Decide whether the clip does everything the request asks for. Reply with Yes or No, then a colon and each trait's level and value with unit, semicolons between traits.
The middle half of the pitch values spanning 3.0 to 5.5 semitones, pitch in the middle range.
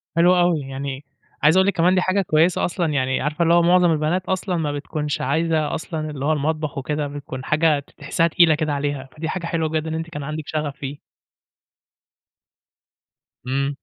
No: narrow, 2.6 semitones; medium, 155 Hz